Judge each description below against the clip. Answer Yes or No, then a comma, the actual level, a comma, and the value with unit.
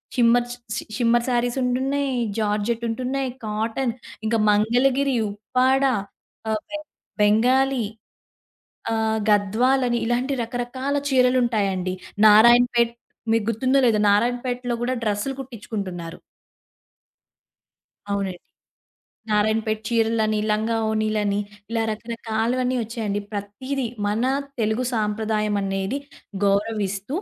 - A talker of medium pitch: No, high, 225 Hz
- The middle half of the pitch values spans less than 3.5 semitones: Yes, average, 2.8 semitones